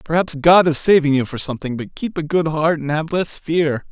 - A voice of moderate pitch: Yes, medium, 155 Hz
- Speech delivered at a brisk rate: Yes, fast, 245 wpm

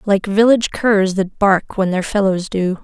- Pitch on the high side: Yes, high, 200 Hz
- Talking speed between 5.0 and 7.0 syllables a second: No, 4.6 syllables/s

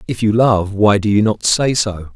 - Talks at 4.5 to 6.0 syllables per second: Yes, 4.6 syllables/s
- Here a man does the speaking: Yes, male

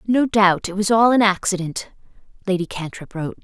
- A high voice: Yes, high, 195 Hz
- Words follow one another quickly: No, average, 175 wpm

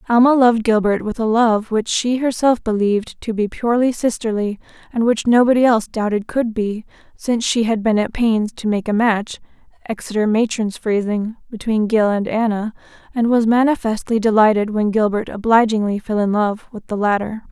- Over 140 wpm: Yes, average, 170 wpm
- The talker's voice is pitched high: Yes, high, 220 Hz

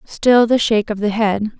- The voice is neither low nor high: No, high, 215 Hz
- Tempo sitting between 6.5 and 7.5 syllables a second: No, 4.9 syllables/s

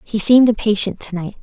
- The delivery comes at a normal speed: No, fast, 210 wpm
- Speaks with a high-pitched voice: Yes, high, 210 Hz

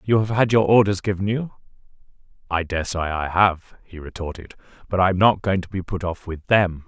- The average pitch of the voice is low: Yes, very low, 95 Hz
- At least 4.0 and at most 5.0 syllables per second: No, 5.5 syllables/s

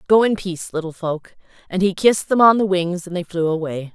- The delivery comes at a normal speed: No, fast, 245 wpm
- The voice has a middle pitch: Yes, medium, 180 Hz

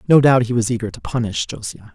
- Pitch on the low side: Yes, low, 120 Hz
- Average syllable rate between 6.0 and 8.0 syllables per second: Yes, 6.7 syllables/s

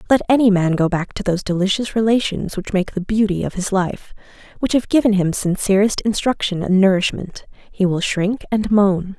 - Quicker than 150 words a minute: Yes, average, 190 wpm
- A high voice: Yes, high, 200 Hz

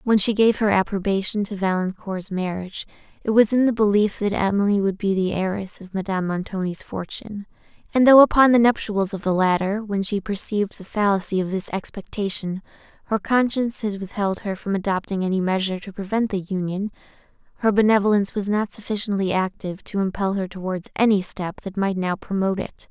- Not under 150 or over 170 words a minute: No, average, 180 wpm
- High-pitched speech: Yes, high, 200 Hz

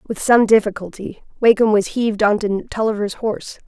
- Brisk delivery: No, average, 165 wpm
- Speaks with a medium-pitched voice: No, high, 210 Hz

